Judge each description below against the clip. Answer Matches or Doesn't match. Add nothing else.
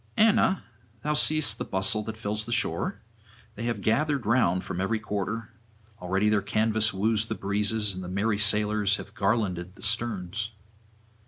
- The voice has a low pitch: Matches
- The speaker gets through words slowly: Doesn't match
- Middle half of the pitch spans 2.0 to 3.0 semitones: Matches